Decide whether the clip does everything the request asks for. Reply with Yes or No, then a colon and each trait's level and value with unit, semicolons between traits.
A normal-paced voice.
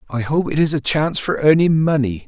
No: fast, 235 wpm